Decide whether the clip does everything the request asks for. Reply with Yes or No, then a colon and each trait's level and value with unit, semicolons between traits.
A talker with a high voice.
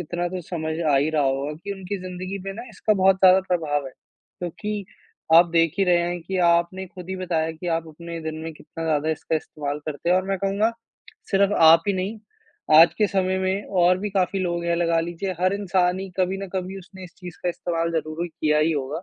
No: medium, 175 Hz